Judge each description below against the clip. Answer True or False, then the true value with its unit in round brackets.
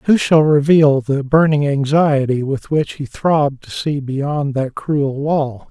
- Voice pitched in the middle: True (145 Hz)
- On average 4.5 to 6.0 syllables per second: False (3.7 syllables/s)